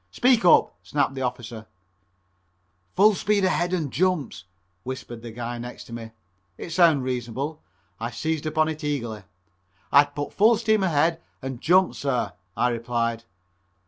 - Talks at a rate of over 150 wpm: No, average, 145 wpm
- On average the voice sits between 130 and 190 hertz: Yes, medium, 140 Hz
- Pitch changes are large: Yes, wide, 6.3 semitones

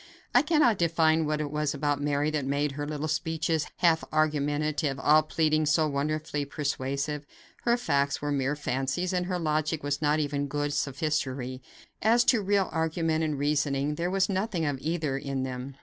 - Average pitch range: No, narrow, 2.2 semitones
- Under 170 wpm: No, average, 175 wpm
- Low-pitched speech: No, medium, 150 Hz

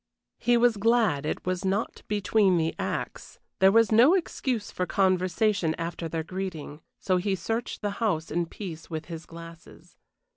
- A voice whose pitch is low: No, medium, 185 Hz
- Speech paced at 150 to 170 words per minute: Yes, average, 160 wpm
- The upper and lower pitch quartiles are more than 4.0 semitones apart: Yes, average, 4.5 semitones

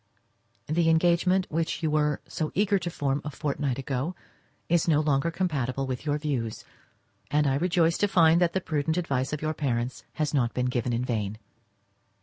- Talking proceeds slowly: No, average, 175 wpm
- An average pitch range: Yes, average, 4.0 semitones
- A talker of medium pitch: Yes, medium, 150 Hz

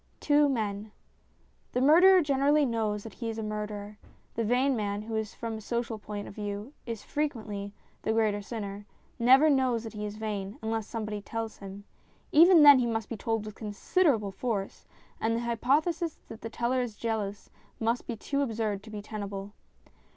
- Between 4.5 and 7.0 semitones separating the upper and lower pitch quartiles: No, average, 3.2 semitones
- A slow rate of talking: No, average, 180 wpm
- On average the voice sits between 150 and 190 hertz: No, high, 225 Hz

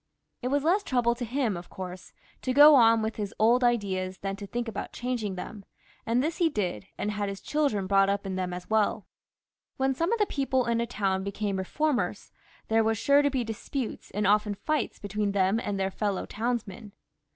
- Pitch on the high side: Yes, high, 220 Hz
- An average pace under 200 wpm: No, fast, 205 wpm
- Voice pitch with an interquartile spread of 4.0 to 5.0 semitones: Yes, average, 4.3 semitones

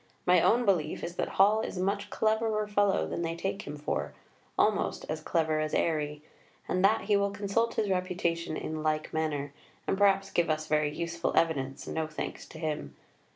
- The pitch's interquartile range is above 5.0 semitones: No, average, 4.4 semitones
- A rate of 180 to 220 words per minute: Yes, average, 190 wpm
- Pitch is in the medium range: Yes, medium, 170 Hz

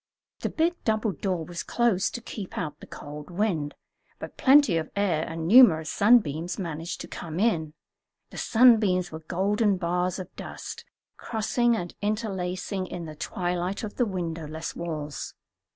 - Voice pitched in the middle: Yes, medium, 180 Hz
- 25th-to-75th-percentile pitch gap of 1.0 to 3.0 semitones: No, average, 4.7 semitones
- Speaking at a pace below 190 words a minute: Yes, average, 150 wpm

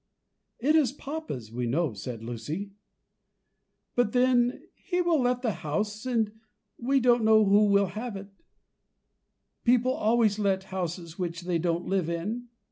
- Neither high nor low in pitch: No, high, 210 Hz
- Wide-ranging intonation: Yes, wide, 6.1 semitones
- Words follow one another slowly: No, average, 145 wpm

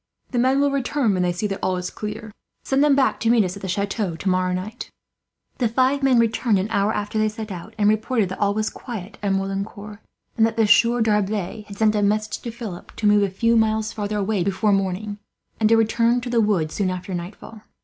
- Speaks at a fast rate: Yes, fast, 230 wpm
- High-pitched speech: Yes, high, 215 Hz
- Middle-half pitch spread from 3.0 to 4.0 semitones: No, narrow, 2.6 semitones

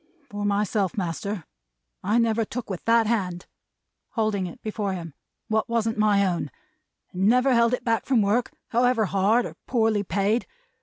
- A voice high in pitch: Yes, high, 215 Hz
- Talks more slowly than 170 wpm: Yes, average, 160 wpm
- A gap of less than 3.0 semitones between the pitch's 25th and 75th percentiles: Yes, narrow, 2.6 semitones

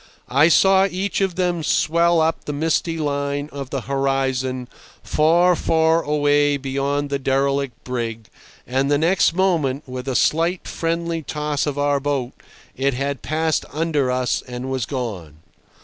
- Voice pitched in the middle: Yes, medium, 145 Hz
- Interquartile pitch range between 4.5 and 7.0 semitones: No, average, 3.5 semitones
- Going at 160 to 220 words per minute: No, average, 150 wpm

